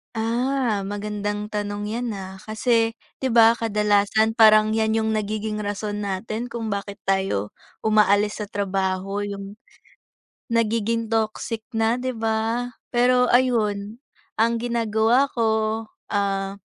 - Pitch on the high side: Yes, high, 215 Hz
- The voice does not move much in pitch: Yes, narrow, 2.0 semitones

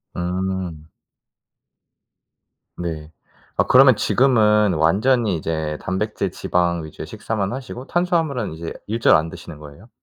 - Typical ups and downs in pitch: No, wide, 6.2 semitones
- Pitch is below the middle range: Yes, very low, 95 Hz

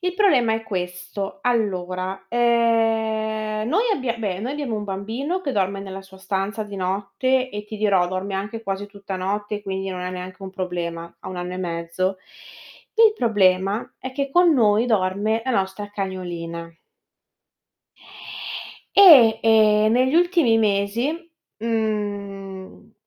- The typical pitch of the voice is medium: No, high, 205 Hz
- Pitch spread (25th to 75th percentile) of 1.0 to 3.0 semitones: No, average, 3.4 semitones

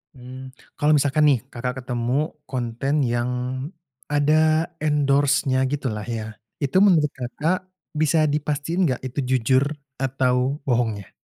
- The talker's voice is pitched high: No, low, 135 Hz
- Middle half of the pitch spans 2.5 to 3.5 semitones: Yes, average, 2.8 semitones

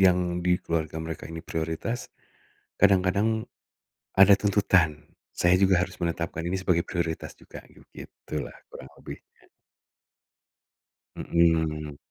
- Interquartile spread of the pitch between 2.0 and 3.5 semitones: Yes, narrow, 2.6 semitones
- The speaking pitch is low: Yes, very low, 85 Hz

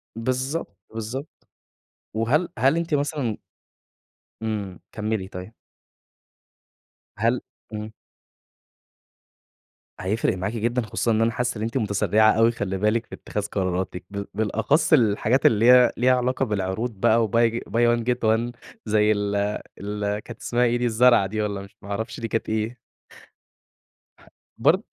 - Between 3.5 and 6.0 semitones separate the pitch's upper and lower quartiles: No, average, 2.7 semitones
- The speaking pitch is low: Yes, low, 110 Hz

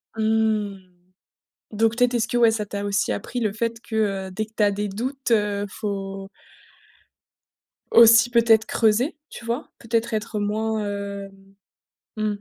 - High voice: Yes, high, 215 Hz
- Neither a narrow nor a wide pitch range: No, narrow, 2.1 semitones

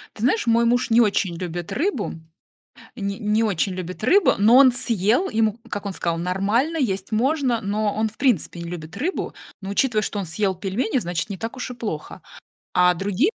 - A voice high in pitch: Yes, high, 215 Hz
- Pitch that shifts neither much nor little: Yes, average, 4.4 semitones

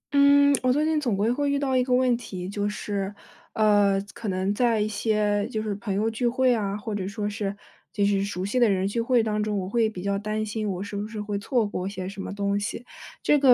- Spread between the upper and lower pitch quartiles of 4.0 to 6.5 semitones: No, average, 3.0 semitones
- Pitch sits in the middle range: No, high, 210 Hz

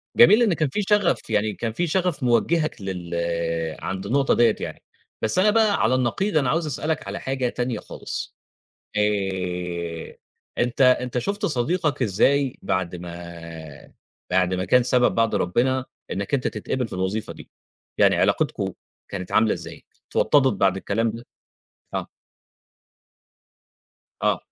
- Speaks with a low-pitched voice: Yes, low, 120 Hz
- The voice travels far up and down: Yes, wide, 6.9 semitones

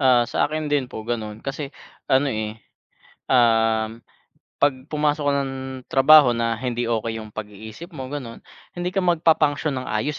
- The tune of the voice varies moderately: Yes, average, 4.6 semitones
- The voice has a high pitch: No, low, 130 Hz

